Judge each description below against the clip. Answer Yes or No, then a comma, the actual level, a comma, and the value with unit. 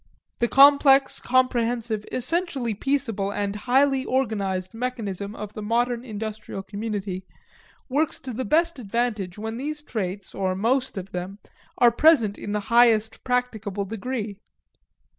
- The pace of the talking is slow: Yes, slow, 130 wpm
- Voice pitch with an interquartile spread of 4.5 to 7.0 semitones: No, average, 4.1 semitones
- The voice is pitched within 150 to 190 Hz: No, high, 225 Hz